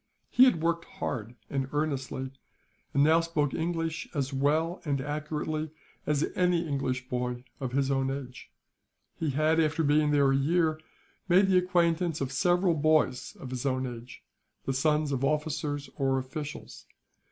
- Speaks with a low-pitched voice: No, medium, 150 Hz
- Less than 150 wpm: No, average, 155 wpm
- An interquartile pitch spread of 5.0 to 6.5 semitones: No, average, 3.2 semitones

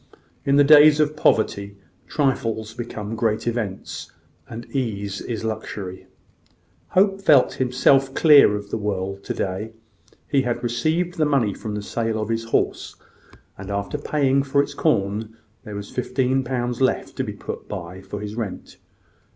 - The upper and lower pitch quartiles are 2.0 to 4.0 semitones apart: No, average, 4.8 semitones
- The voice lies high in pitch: No, low, 115 Hz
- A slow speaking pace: No, average, 160 wpm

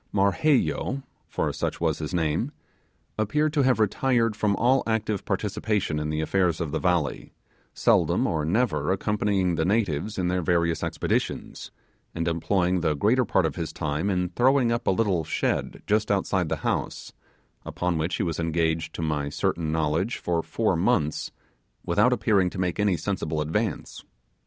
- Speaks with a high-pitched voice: No, very low, 90 Hz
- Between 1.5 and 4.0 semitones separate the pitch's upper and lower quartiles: No, average, 4.7 semitones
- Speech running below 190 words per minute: Yes, average, 165 wpm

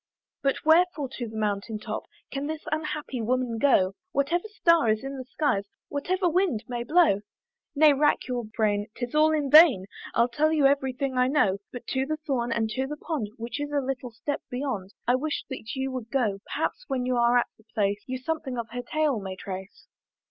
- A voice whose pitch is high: Yes, very high, 260 Hz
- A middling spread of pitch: Yes, average, 4.5 semitones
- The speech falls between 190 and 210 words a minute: Yes, fast, 205 wpm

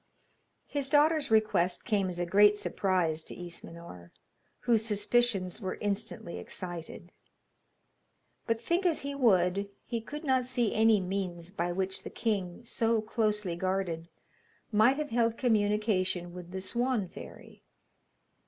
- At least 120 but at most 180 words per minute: Yes, slow, 135 wpm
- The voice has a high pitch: Yes, high, 205 Hz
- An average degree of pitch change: Yes, average, 4.3 semitones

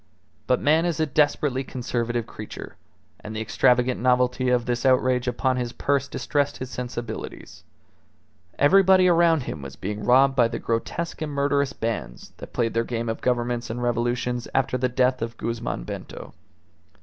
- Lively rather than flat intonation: No, average, 2.8 semitones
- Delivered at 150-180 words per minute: Yes, average, 160 wpm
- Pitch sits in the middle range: No, low, 125 Hz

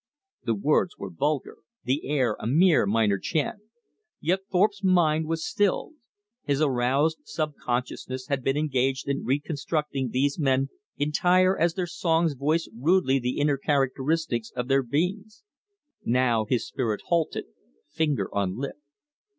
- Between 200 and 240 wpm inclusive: No, slow, 135 wpm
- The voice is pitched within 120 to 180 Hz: Yes, medium, 140 Hz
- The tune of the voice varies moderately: Yes, average, 4.3 semitones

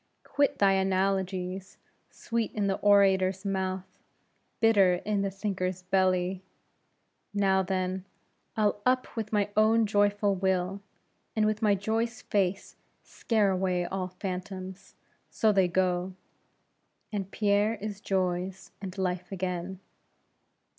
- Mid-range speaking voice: No, high, 195 Hz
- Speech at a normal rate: No, slow, 120 wpm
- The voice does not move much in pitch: Yes, narrow, 1.8 semitones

